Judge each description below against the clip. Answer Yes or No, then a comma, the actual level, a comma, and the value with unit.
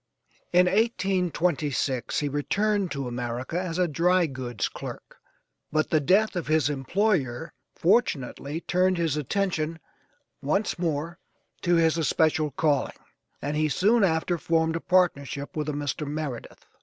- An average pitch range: Yes, average, 3.9 semitones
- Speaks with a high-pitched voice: No, medium, 160 Hz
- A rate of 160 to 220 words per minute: No, slow, 135 wpm